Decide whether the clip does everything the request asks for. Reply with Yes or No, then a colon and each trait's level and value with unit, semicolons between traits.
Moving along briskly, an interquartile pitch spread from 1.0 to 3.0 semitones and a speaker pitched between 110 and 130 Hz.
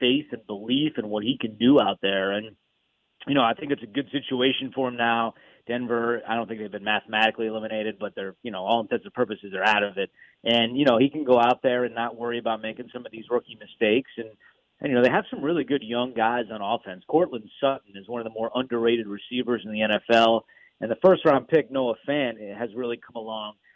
Yes: fast, 240 wpm; narrow, 2.4 semitones; low, 115 Hz